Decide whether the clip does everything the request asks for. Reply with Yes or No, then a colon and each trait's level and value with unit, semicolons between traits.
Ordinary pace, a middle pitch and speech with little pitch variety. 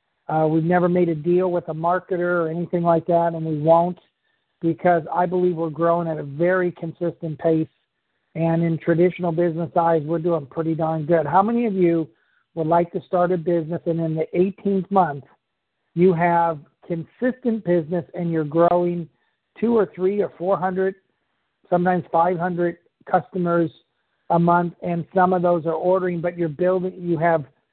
Yes: average, 170 wpm; medium, 175 Hz; narrow, 1.5 semitones